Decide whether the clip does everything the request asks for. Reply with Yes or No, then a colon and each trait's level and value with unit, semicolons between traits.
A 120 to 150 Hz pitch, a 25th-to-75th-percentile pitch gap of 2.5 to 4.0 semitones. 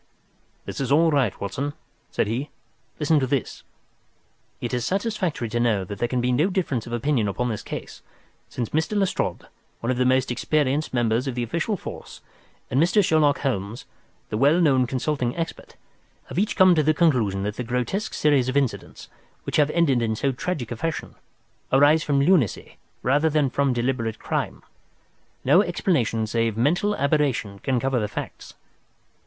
No: low, 135 Hz; average, 4.5 semitones